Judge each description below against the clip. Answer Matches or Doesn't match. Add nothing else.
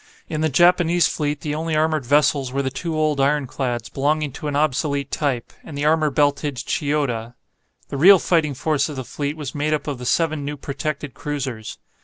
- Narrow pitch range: Matches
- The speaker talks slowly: Doesn't match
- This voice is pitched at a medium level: Matches